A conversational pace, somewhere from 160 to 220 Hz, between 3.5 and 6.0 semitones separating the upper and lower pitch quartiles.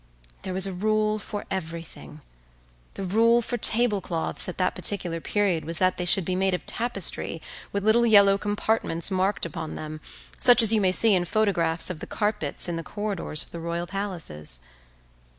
Yes: average, 180 wpm; high, 190 Hz; average, 3.8 semitones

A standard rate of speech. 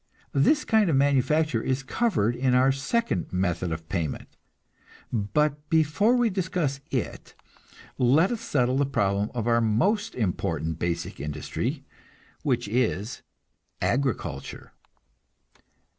No: slow, 115 wpm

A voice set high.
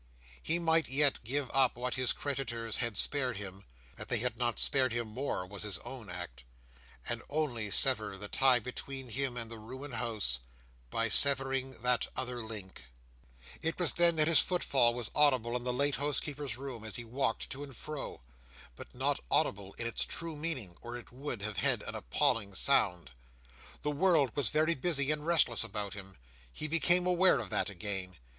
No: low, 125 Hz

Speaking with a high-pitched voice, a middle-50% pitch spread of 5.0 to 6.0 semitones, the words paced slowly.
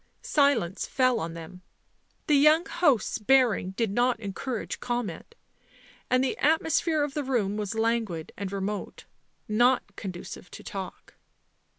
Yes: high, 230 Hz; wide, 5.4 semitones; slow, 130 wpm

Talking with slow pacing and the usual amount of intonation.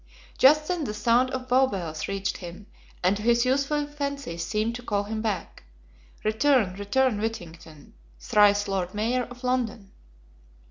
No: average, 150 wpm; average, 4.6 semitones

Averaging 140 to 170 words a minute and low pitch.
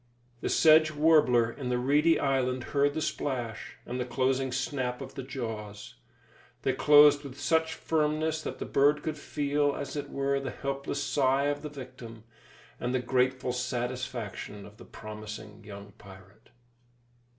Yes: average, 155 wpm; low, 130 Hz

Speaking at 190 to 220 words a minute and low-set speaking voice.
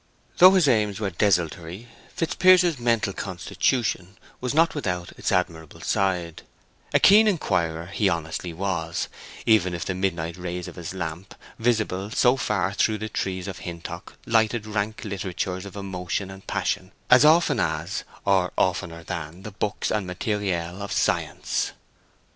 No: average, 150 wpm; very low, 95 Hz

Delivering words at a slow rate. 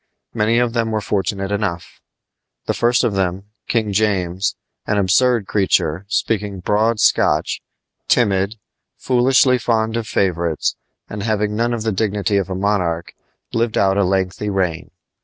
No: average, 145 wpm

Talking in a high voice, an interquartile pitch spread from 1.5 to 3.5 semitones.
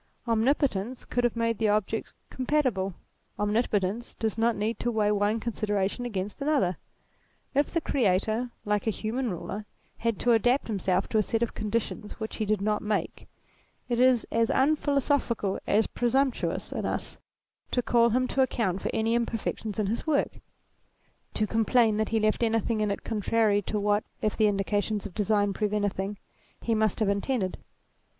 Yes: high, 220 Hz; narrow, 2.4 semitones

